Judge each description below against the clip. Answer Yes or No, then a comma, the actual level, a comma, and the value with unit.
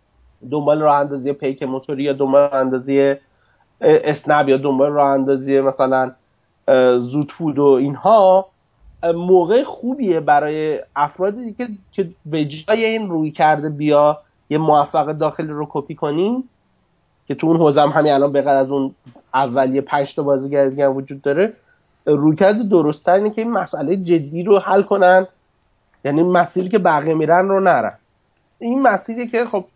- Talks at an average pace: Yes, average, 145 wpm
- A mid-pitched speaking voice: Yes, medium, 150 Hz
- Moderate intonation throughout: Yes, average, 4.8 semitones